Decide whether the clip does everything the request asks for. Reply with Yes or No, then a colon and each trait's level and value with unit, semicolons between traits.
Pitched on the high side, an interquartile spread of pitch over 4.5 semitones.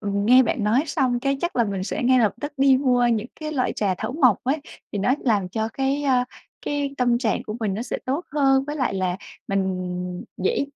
Yes: high, 245 Hz; average, 5.1 semitones